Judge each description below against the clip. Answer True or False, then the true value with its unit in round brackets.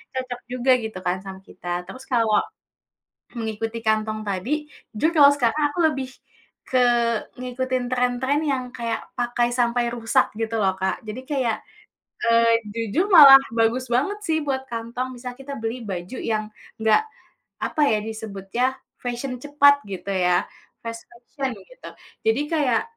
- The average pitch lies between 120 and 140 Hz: False (240 Hz)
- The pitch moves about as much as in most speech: True (3.0 semitones)